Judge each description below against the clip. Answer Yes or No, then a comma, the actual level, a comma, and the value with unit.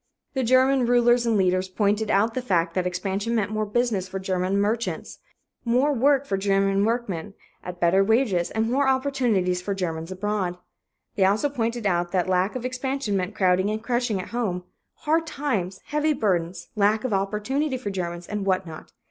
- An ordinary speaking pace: Yes, average, 180 wpm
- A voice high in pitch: Yes, high, 205 Hz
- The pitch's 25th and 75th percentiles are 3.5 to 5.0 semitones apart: Yes, average, 4.6 semitones